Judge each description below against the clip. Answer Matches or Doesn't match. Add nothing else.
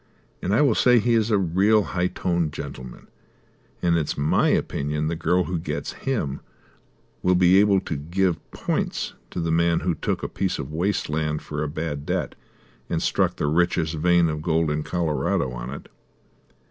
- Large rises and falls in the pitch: Doesn't match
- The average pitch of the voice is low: Matches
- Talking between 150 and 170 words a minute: Doesn't match